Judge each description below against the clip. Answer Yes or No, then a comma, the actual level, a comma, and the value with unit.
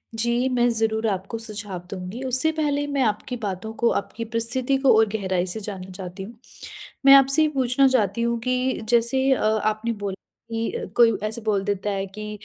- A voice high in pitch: Yes, high, 225 Hz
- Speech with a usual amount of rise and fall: Yes, average, 3.5 semitones